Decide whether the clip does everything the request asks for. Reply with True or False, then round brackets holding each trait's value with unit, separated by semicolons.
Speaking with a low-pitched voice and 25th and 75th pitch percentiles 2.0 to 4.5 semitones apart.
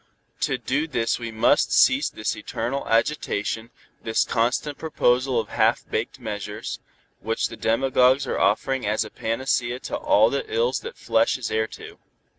True (120 Hz; 3.7 semitones)